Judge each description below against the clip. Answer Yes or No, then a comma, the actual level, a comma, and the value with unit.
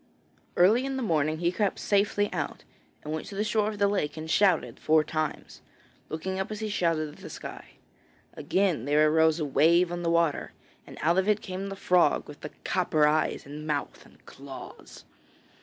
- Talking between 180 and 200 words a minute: Yes, average, 195 wpm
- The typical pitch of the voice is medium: Yes, medium, 170 Hz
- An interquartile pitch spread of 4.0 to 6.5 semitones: Yes, average, 4.4 semitones